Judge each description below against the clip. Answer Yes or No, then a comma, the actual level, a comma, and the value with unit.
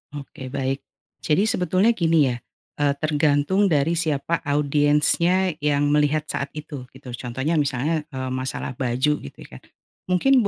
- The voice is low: No, medium, 145 Hz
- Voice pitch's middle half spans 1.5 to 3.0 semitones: No, average, 3.4 semitones